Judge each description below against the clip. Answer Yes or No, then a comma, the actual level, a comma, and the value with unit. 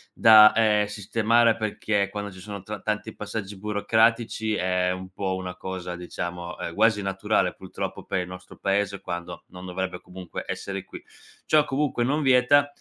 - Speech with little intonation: No, average, 3.2 semitones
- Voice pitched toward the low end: Yes, low, 100 Hz